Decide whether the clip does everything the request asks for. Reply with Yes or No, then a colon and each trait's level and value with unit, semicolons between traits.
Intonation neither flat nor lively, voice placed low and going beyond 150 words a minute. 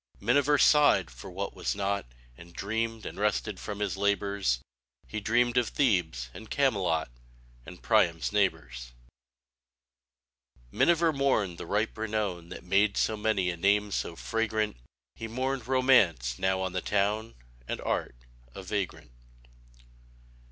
No: average, 3.8 semitones; low, 105 Hz; slow, 135 wpm